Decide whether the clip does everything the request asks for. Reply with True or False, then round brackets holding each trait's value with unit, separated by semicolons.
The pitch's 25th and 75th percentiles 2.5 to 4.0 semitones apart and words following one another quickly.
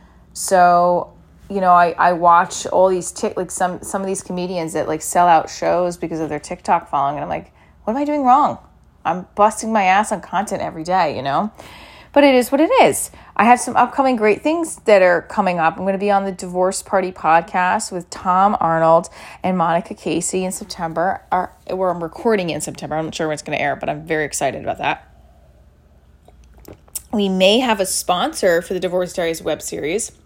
True (3.3 semitones; 215 wpm)